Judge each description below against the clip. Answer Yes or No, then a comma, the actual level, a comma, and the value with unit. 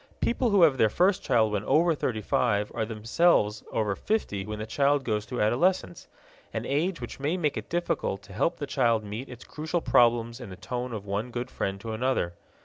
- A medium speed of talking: No, fast, 210 wpm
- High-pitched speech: No, low, 120 Hz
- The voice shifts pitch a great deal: Yes, wide, 5.9 semitones